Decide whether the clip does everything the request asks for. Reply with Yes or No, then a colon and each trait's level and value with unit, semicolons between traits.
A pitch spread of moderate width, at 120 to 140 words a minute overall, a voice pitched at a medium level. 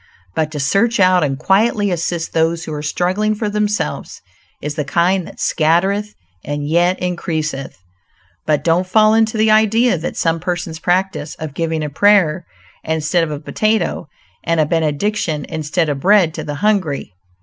No: average, 4.7 semitones; average, 165 wpm; medium, 170 Hz